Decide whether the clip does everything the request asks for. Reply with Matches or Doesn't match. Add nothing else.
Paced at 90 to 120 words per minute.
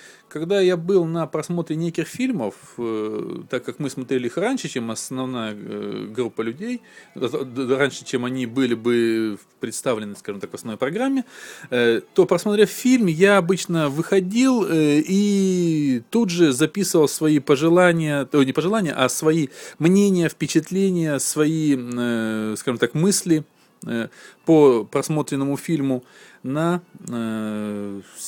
Matches